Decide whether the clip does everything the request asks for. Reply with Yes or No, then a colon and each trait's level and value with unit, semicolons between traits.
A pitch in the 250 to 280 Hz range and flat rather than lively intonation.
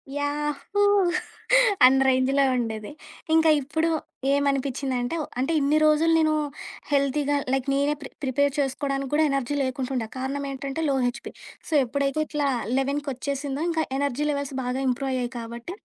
Yes: very high, 275 Hz; narrow, 1.9 semitones